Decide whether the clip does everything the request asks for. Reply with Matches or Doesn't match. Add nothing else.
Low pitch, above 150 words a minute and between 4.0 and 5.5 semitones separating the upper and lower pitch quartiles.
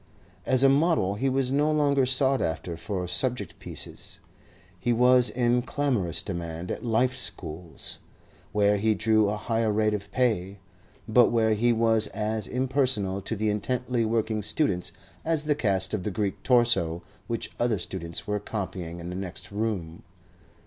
Matches